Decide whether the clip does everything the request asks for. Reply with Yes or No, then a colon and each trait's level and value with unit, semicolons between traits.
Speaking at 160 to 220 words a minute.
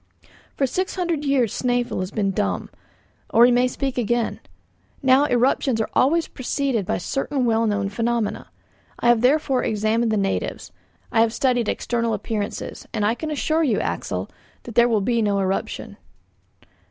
Yes: average, 165 wpm